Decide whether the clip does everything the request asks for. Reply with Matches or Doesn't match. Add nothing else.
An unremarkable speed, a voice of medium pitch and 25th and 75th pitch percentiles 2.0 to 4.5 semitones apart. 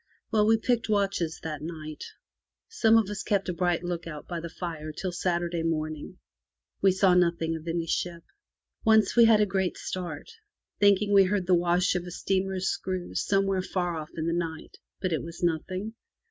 Matches